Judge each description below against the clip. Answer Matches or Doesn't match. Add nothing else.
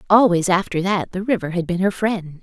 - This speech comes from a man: Doesn't match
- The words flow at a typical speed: Doesn't match